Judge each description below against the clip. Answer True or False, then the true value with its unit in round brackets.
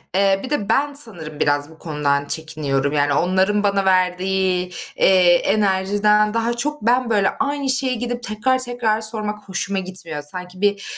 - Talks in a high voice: True (195 Hz)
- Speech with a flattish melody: False (4.1 semitones)